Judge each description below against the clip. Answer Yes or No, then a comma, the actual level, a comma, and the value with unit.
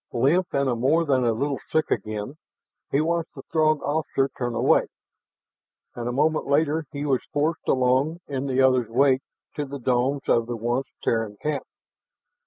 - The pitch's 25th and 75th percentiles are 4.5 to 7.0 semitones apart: No, average, 3.4 semitones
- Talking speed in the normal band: Yes, average, 170 wpm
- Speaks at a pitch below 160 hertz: Yes, low, 135 Hz